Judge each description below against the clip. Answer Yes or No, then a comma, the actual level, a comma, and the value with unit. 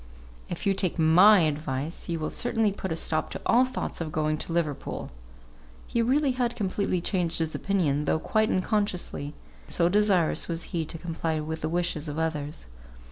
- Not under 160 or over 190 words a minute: Yes, average, 180 wpm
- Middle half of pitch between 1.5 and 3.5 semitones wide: No, average, 4.3 semitones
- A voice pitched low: No, medium, 170 Hz